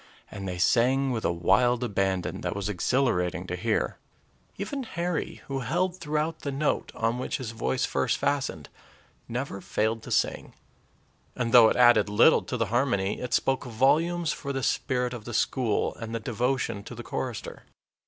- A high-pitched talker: No, low, 120 Hz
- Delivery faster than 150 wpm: Yes, average, 175 wpm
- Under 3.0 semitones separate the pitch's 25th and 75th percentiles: No, average, 4.1 semitones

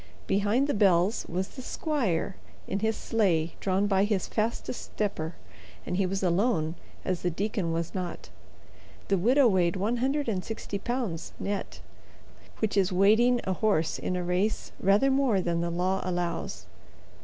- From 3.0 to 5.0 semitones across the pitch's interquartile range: Yes, average, 3.6 semitones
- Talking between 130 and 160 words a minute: Yes, average, 155 wpm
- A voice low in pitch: No, high, 195 Hz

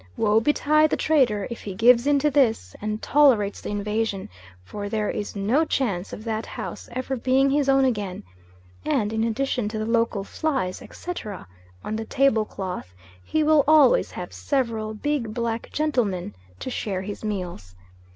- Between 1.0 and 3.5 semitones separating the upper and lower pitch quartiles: No, average, 4.8 semitones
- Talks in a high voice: Yes, high, 225 Hz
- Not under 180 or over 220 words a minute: No, average, 170 wpm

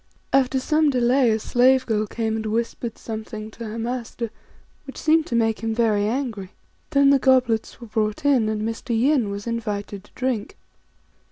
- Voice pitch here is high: Yes, high, 230 Hz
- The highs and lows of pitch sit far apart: No, average, 3.0 semitones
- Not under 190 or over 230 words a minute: No, average, 175 wpm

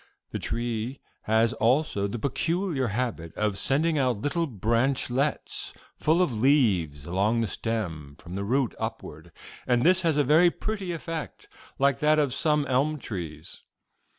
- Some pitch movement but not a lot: No, wide, 5.9 semitones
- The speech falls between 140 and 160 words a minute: Yes, average, 150 wpm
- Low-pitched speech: Yes, low, 125 Hz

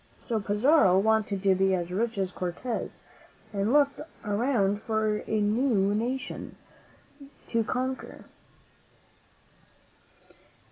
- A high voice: Yes, high, 215 Hz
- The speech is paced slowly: Yes, slow, 105 wpm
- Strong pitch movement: No, average, 3.5 semitones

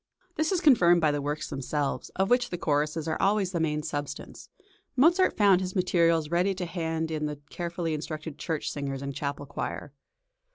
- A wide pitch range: No, average, 3.7 semitones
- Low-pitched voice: No, medium, 165 Hz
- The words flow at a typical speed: Yes, average, 180 wpm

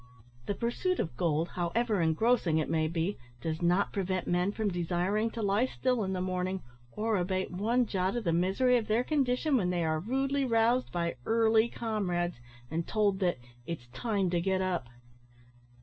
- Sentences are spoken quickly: No, average, 180 wpm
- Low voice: No, high, 190 Hz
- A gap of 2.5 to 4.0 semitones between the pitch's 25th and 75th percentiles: No, average, 4.7 semitones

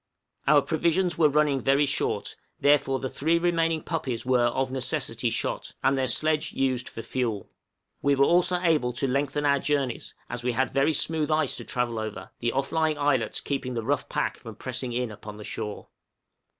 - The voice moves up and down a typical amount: Yes, average, 3.6 semitones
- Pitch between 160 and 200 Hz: No, low, 135 Hz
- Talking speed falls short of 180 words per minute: No, average, 190 wpm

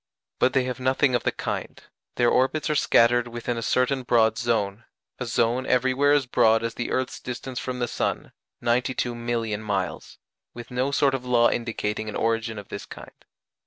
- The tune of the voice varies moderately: No, narrow, 1.9 semitones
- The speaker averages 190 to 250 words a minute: No, average, 180 wpm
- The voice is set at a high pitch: No, low, 120 Hz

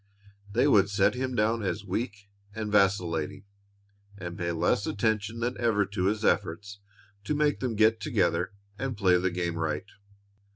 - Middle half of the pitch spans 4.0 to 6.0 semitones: No, average, 3.2 semitones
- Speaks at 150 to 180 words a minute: Yes, average, 160 wpm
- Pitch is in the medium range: No, low, 100 Hz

